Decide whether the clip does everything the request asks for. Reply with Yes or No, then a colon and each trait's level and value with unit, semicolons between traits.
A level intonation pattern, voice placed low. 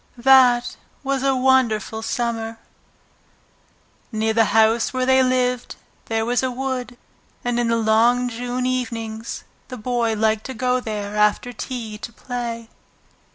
No: narrow, 2.2 semitones; high, 240 Hz